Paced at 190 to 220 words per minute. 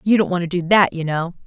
No: fast, 330 wpm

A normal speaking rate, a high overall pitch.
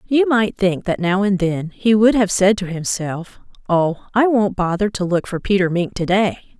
No: fast, 220 wpm; high, 195 Hz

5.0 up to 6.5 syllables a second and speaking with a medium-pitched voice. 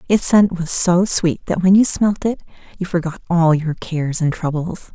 No: 4.7 syllables/s; medium, 175 Hz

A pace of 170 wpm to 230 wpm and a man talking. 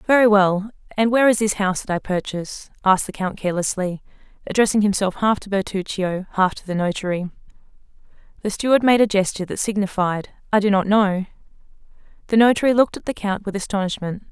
No: average, 175 wpm; female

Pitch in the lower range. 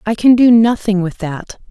No: high, 210 Hz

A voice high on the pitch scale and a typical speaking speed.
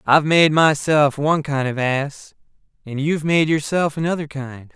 No: medium, 150 Hz; average, 165 wpm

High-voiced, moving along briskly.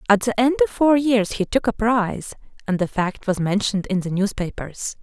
Yes: high, 215 Hz; fast, 215 wpm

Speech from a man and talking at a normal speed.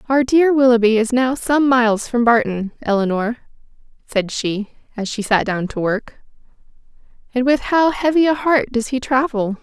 No: female; average, 170 wpm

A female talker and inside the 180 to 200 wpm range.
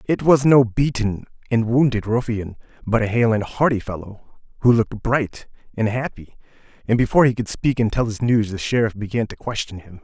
No: male; average, 195 wpm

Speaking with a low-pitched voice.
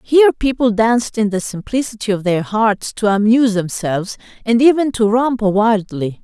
No: high, 220 Hz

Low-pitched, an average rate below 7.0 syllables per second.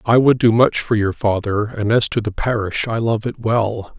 Yes: low, 110 Hz; 4.7 syllables/s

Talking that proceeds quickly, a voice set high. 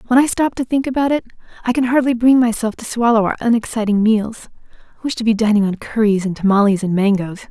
Yes: fast, 225 wpm; high, 225 Hz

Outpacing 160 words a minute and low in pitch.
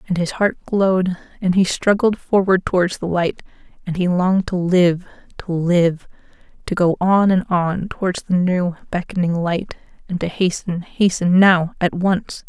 No: average, 170 wpm; medium, 180 Hz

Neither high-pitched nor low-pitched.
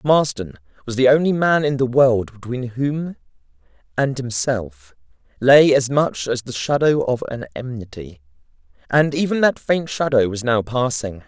No: low, 125 Hz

